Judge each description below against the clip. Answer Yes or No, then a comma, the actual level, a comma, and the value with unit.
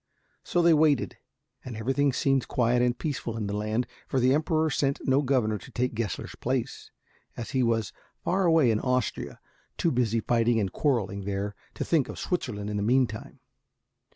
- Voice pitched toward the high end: No, low, 125 Hz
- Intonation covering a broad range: No, average, 4.0 semitones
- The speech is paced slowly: No, average, 180 wpm